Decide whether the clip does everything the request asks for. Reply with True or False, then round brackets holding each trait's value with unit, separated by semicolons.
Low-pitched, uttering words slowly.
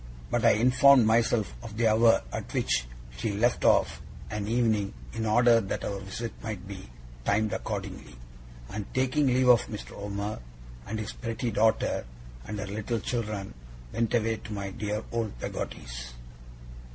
False (110 Hz; 155 wpm)